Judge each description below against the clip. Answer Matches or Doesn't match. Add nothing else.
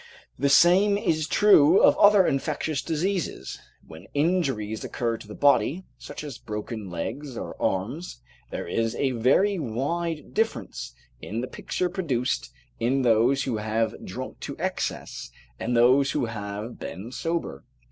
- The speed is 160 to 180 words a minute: Doesn't match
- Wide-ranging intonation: Matches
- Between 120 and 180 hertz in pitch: Matches